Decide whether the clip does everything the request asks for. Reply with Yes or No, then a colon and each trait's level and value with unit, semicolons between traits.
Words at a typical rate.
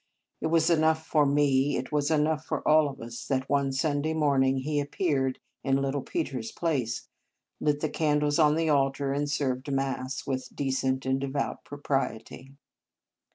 Yes: average, 165 wpm